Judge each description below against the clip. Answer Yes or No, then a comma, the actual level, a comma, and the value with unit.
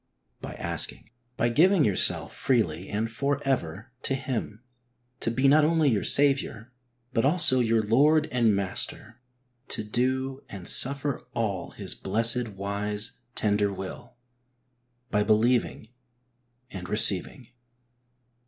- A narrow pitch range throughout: No, average, 4.5 semitones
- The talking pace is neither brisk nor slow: No, slow, 120 wpm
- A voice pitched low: Yes, low, 115 Hz